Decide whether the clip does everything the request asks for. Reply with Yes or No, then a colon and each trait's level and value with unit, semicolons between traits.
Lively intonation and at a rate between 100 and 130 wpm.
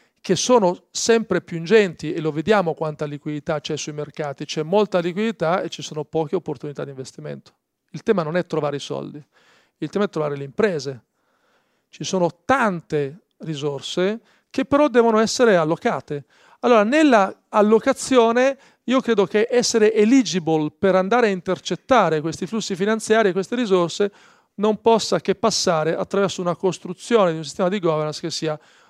No: wide, 5.9 semitones; average, 160 wpm